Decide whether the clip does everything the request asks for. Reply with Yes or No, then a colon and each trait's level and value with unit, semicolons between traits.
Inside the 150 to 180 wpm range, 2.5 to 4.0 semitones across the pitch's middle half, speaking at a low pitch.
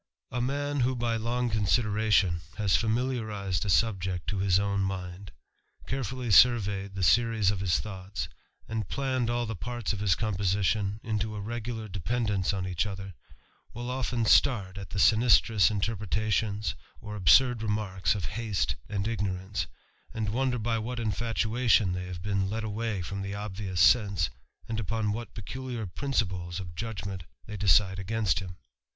Yes: average, 155 wpm; average, 3.1 semitones; low, 105 Hz